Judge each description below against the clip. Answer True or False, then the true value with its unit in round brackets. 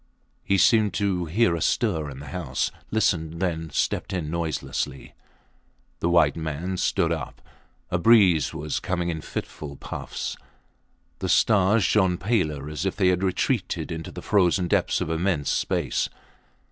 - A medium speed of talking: True (150 wpm)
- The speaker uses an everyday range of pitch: True (3.5 semitones)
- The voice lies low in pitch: True (85 Hz)